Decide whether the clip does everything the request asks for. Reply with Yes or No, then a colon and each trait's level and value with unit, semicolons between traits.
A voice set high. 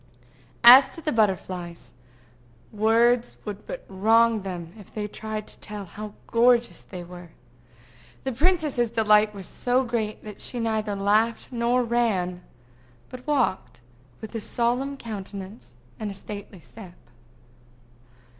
Yes: high, 220 Hz